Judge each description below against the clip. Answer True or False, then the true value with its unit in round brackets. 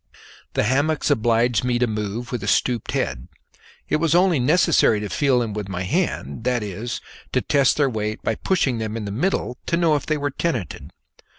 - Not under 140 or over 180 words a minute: False (200 wpm)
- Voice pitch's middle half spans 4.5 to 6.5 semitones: True (5.2 semitones)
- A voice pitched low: True (120 Hz)